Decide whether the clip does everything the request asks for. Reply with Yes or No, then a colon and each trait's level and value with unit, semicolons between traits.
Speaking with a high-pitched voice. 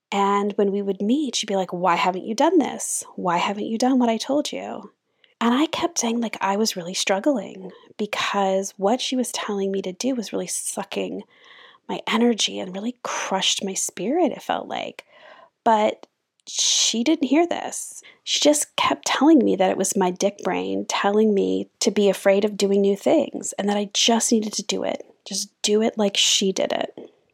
Yes: high, 215 Hz